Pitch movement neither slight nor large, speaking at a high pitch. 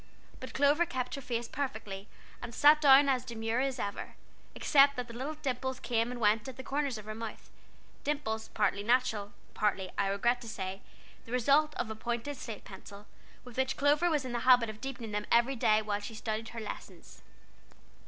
Yes: average, 3.7 semitones; high, 240 Hz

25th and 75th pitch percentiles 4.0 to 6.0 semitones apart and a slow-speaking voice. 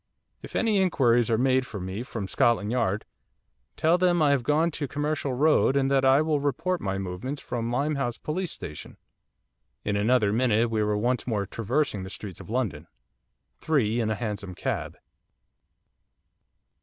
No: wide, 5.5 semitones; average, 170 wpm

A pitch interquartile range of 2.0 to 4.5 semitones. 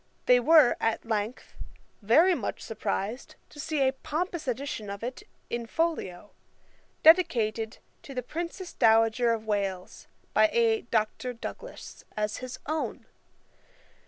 No: average, 5.2 semitones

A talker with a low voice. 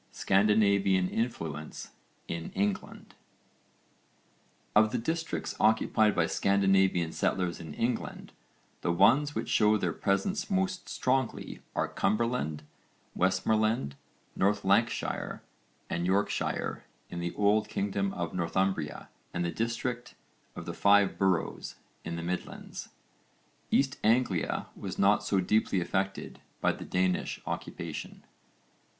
Yes: low, 100 Hz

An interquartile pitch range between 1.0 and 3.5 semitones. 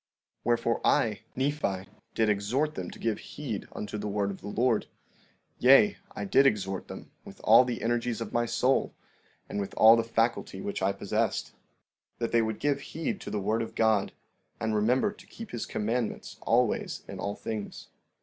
Yes: average, 3.2 semitones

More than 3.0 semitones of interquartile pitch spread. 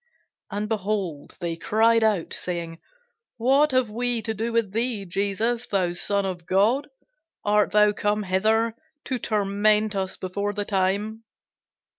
No: narrow, 2.6 semitones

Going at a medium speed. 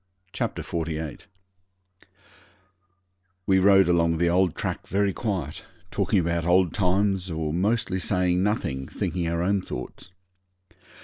No: slow, 120 wpm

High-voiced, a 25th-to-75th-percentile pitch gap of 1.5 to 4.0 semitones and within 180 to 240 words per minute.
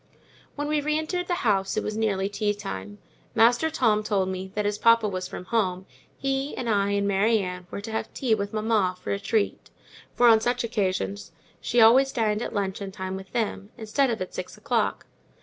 Yes: high, 210 Hz; average, 3.1 semitones; fast, 205 wpm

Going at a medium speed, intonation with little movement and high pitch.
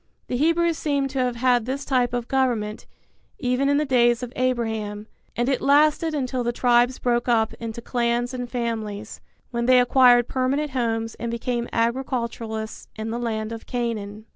Yes: average, 170 wpm; narrow, 2.1 semitones; high, 240 Hz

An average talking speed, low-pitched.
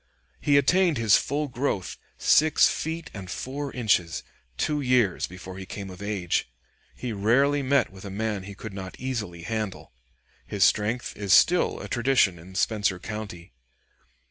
Yes: average, 155 wpm; low, 110 Hz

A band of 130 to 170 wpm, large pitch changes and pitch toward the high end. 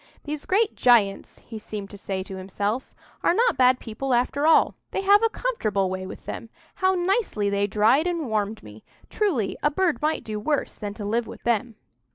No: average, 200 wpm; wide, 8.0 semitones; high, 235 Hz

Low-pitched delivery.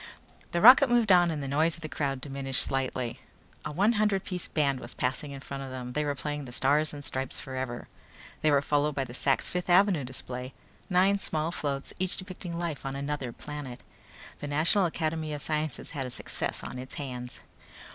No: medium, 145 Hz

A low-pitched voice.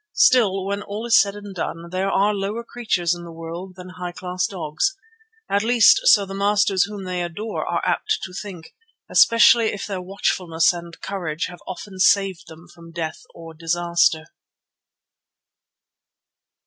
No: medium, 185 Hz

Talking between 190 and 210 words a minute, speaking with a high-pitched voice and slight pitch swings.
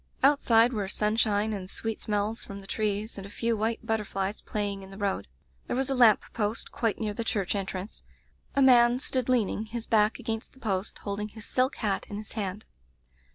Yes: average, 200 wpm; high, 215 Hz; narrow, 2.3 semitones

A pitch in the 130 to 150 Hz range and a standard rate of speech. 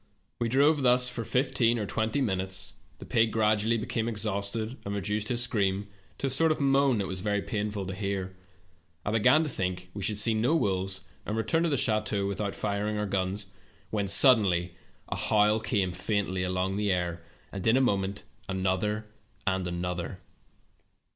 No: low, 105 Hz; average, 180 wpm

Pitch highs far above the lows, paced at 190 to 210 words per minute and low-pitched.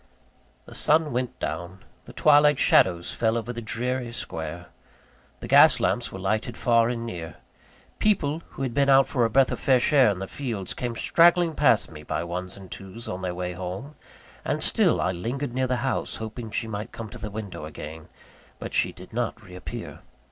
Yes: wide, 5.9 semitones; average, 200 wpm; low, 115 Hz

